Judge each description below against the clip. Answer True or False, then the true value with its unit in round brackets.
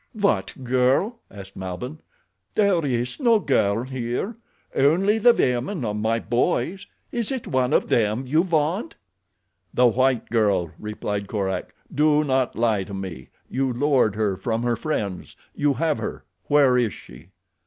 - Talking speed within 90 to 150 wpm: True (145 wpm)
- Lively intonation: True (6.4 semitones)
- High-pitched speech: False (125 Hz)